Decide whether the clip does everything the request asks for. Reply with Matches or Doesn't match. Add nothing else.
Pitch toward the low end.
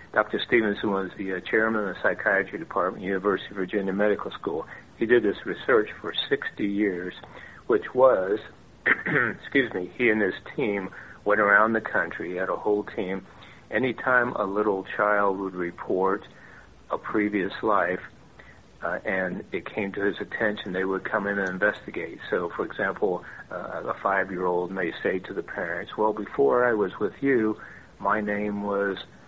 Matches